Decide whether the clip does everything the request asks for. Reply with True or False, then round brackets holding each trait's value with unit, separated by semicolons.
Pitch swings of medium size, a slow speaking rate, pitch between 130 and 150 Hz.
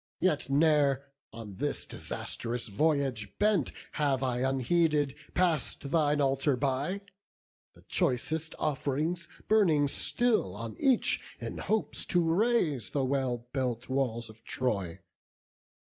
True (4.4 semitones; 115 wpm; 140 Hz)